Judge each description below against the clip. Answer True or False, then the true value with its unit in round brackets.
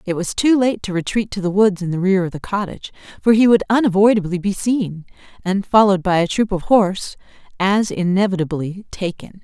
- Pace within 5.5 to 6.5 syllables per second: True (5.7 syllables/s)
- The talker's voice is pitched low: False (195 Hz)